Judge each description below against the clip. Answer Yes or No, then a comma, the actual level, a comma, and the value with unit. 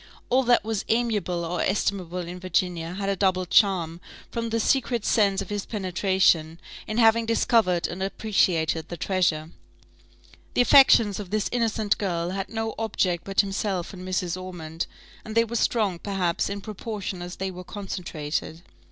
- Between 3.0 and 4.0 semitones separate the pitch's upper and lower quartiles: Yes, average, 3.4 semitones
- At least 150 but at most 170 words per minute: Yes, average, 160 wpm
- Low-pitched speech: No, high, 195 Hz